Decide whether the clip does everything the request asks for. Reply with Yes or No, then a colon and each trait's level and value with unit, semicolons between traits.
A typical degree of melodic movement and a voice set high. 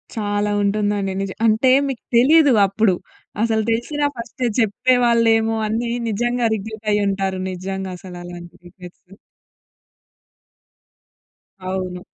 Yes: average, 3.4 semitones; high, 210 Hz